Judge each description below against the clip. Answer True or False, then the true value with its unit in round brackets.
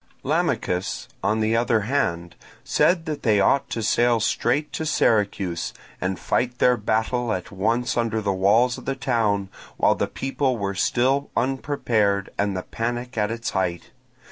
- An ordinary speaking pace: True (160 wpm)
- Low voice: True (115 Hz)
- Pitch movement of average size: True (3.7 semitones)